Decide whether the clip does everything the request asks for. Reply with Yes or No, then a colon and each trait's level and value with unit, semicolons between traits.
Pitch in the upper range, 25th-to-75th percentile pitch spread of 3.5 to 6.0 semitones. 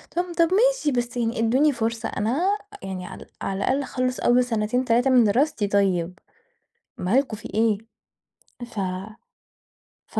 Yes: high, 240 Hz; average, 4.1 semitones